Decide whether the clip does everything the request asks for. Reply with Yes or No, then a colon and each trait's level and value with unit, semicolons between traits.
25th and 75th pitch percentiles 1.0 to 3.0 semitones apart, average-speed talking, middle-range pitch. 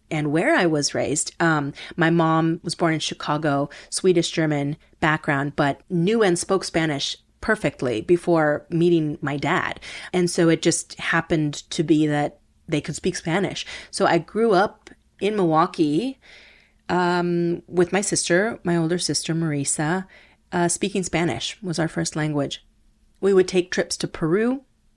Yes: average, 2.7 semitones; average, 155 wpm; medium, 170 Hz